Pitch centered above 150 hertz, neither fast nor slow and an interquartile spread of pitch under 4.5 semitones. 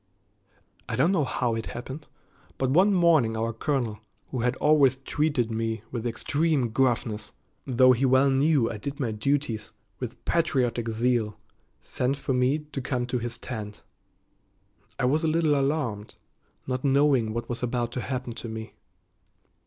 No: low, 125 Hz; average, 160 wpm; average, 3.5 semitones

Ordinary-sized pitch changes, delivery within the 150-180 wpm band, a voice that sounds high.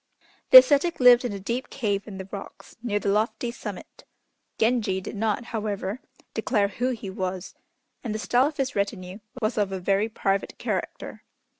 Yes: average, 3.6 semitones; average, 175 wpm; high, 215 Hz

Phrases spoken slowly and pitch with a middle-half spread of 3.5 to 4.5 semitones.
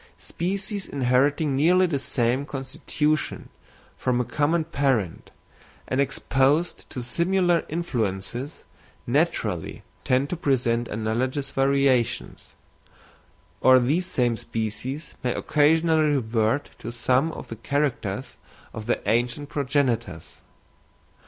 Yes: slow, 105 wpm; average, 4.0 semitones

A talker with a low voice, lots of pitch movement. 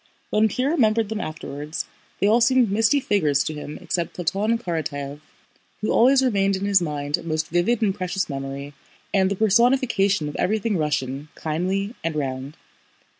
No: high, 190 Hz; wide, 6.3 semitones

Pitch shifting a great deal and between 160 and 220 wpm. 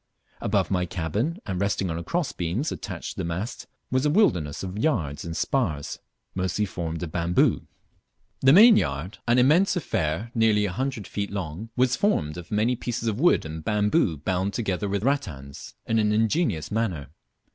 Yes: wide, 6.6 semitones; average, 170 wpm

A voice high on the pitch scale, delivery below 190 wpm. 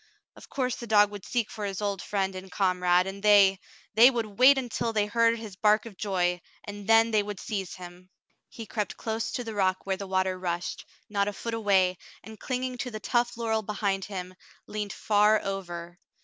No: high, 205 Hz; fast, 205 wpm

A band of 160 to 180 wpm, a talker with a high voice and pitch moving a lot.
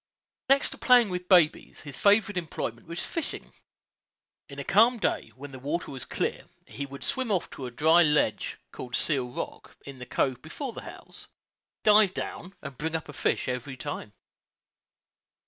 No: average, 175 wpm; medium, 160 Hz; wide, 7.4 semitones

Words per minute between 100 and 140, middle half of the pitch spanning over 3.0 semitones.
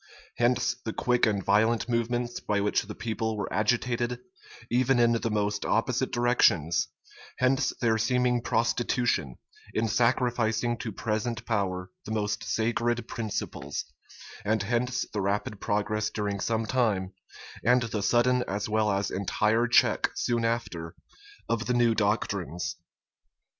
No: slow, 135 wpm; narrow, 2.5 semitones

